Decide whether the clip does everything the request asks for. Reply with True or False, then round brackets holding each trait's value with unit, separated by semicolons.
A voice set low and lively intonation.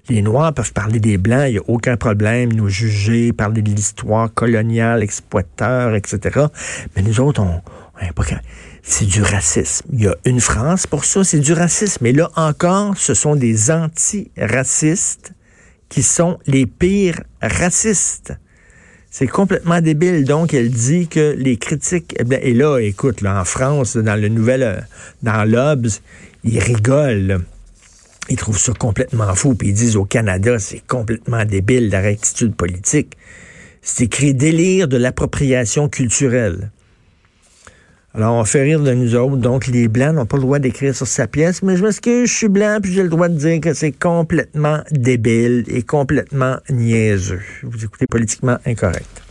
True (125 Hz; 5.7 semitones)